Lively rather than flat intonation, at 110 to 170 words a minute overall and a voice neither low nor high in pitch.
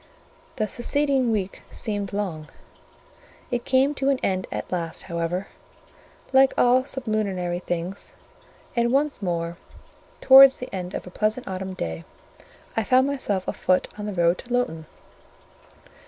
No: wide, 6.0 semitones; average, 140 wpm; high, 205 Hz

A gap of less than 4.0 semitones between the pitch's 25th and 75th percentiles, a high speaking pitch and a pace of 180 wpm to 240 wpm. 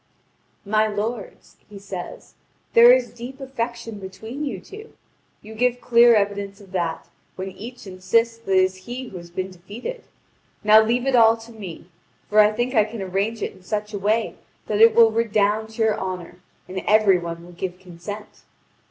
Yes: average, 3.5 semitones; high, 215 Hz; average, 185 wpm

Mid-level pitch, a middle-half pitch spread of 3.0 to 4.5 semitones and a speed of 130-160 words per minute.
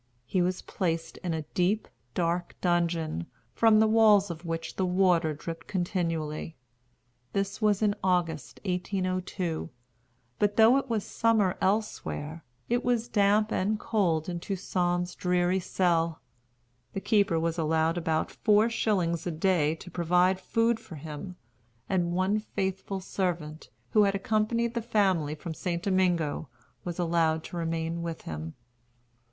Yes: medium, 180 Hz; average, 3.5 semitones; average, 140 wpm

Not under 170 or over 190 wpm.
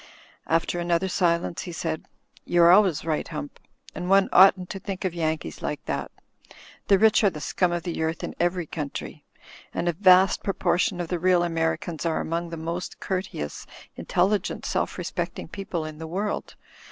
Yes: average, 175 wpm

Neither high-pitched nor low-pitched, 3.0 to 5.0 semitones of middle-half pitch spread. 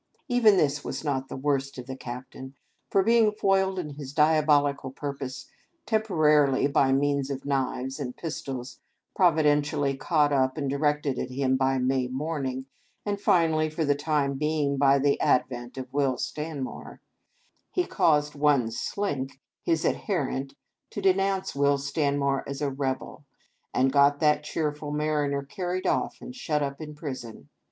No: medium, 145 Hz; narrow, 2.6 semitones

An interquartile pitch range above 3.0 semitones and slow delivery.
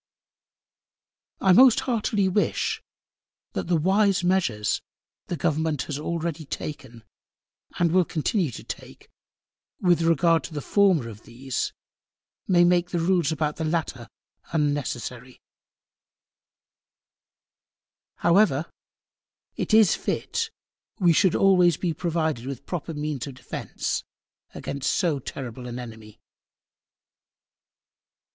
Yes: average, 4.6 semitones; slow, 110 wpm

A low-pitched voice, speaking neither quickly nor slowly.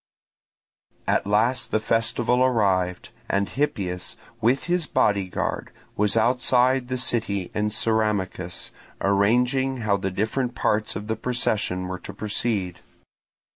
No: low, 110 Hz; slow, 125 wpm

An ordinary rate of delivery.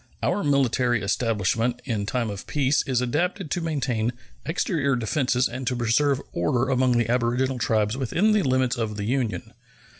Yes: average, 160 wpm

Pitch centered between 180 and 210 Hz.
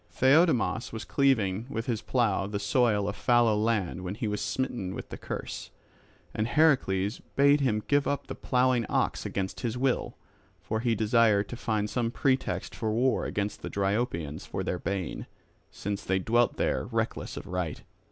No: low, 110 Hz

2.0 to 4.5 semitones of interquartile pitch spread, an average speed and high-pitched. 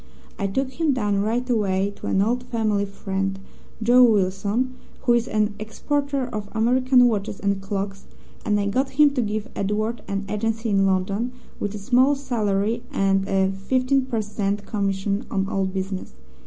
Yes: average, 3.8 semitones; average, 170 wpm; high, 210 Hz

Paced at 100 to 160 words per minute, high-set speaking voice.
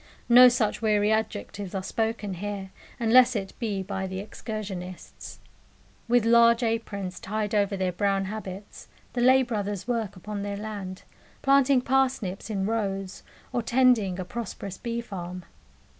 Yes: average, 145 wpm; high, 210 Hz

